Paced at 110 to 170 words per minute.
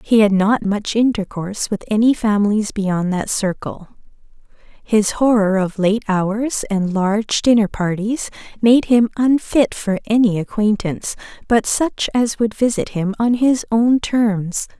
Yes: average, 145 wpm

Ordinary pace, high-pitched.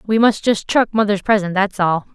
No: fast, 225 wpm; high, 205 Hz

